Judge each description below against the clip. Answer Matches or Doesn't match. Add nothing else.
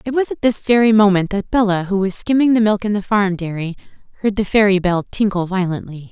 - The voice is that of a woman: Matches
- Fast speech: Matches